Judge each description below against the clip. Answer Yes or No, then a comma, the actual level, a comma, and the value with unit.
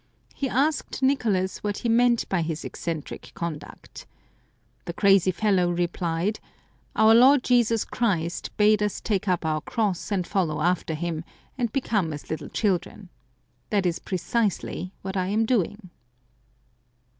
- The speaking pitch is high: Yes, high, 195 Hz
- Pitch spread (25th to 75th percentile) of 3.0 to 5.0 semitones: Yes, average, 4.5 semitones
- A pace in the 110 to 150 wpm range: Yes, average, 145 wpm